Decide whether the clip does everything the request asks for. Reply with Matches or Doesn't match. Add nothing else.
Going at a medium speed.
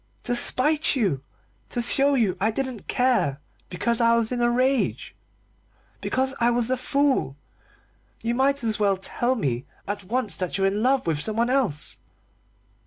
Matches